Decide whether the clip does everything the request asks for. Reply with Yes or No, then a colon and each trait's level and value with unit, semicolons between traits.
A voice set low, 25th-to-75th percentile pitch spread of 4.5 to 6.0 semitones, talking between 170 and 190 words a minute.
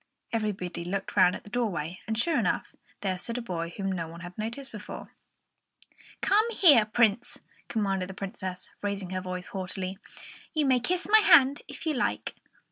No: high, 205 Hz; average, 4.9 semitones; average, 175 wpm